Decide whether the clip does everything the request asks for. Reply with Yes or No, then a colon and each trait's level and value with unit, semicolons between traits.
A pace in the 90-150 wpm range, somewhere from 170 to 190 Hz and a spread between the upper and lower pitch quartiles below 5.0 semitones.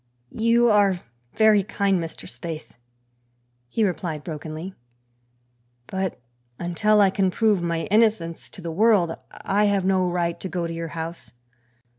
Yes: average, 140 wpm; medium, 185 Hz; average, 3.7 semitones